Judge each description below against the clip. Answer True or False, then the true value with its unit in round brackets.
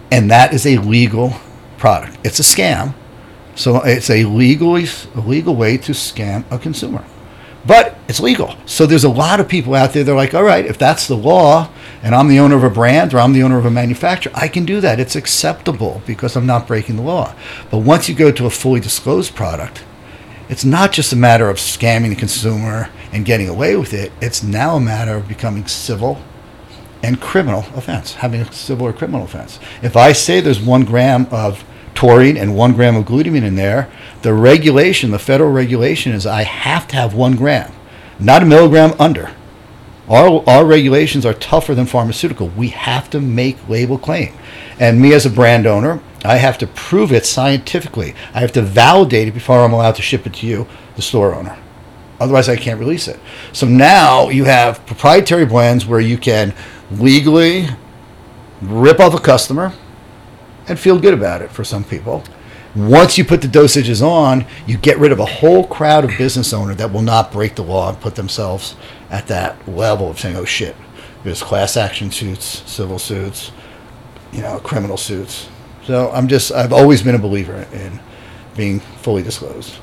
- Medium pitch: False (120 Hz)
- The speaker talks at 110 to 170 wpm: False (195 wpm)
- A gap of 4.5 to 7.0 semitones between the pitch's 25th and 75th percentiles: False (3.9 semitones)